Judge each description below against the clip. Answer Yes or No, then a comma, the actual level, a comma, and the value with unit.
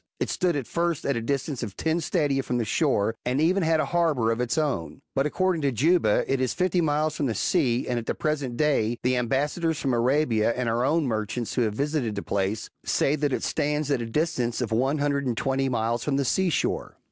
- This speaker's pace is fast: Yes, fast, 240 wpm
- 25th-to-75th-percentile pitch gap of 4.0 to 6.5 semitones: Yes, average, 4.5 semitones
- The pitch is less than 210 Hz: Yes, low, 135 Hz